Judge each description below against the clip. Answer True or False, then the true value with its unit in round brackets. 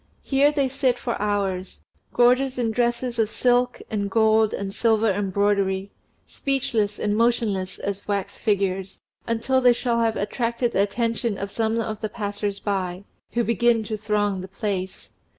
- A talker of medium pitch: False (220 Hz)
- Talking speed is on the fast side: False (155 wpm)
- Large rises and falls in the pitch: False (2.9 semitones)